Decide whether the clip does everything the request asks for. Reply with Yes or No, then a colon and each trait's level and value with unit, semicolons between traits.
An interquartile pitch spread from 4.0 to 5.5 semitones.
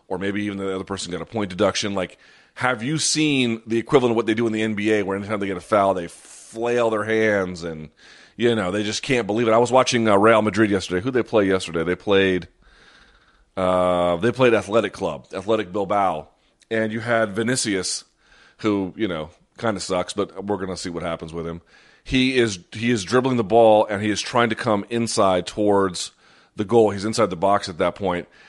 No: average, 3.4 semitones